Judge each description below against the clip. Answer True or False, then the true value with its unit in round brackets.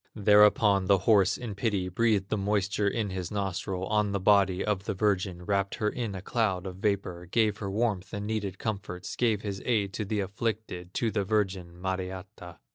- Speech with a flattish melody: True (2.2 semitones)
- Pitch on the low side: True (100 Hz)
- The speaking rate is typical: True (190 wpm)